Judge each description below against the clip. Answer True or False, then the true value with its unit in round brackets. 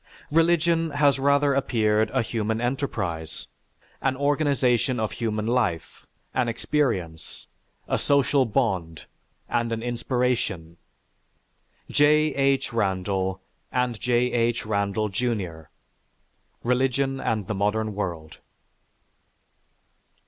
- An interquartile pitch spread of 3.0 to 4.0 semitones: False (4.7 semitones)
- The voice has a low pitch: True (120 Hz)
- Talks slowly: True (100 wpm)